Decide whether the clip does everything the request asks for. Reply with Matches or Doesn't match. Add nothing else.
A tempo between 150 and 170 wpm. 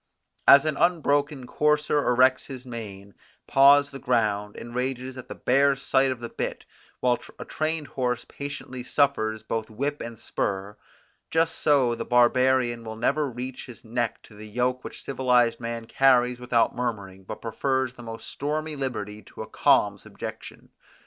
Matches